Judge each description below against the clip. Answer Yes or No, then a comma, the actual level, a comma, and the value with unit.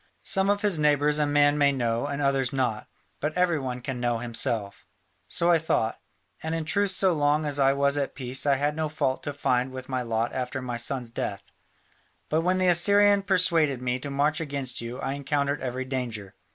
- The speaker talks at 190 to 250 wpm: Yes, fast, 205 wpm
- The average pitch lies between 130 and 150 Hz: Yes, medium, 140 Hz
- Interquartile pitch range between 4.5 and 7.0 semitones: No, average, 3.5 semitones